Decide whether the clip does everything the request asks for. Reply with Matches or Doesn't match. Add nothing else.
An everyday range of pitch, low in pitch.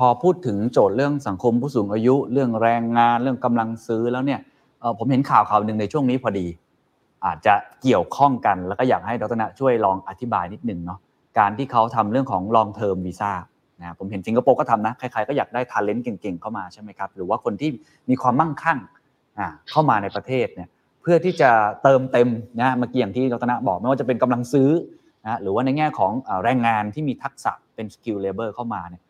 Matches